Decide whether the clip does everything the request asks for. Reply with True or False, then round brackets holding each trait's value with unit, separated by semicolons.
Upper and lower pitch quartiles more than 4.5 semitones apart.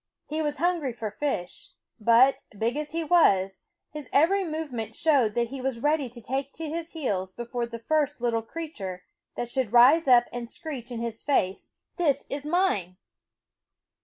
True (5.0 semitones)